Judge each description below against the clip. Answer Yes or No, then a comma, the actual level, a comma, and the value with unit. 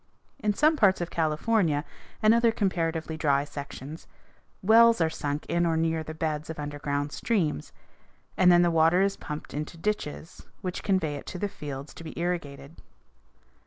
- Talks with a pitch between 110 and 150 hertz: No, medium, 165 Hz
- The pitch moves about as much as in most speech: Yes, average, 4.1 semitones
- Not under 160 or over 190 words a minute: Yes, average, 165 wpm